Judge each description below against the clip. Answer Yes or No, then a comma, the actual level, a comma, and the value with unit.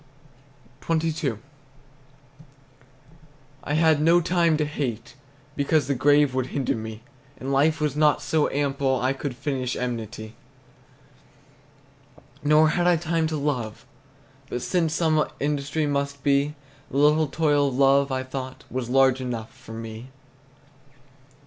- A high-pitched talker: No, medium, 140 Hz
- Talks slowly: Yes, slow, 130 wpm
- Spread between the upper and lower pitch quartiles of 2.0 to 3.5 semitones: Yes, average, 2.9 semitones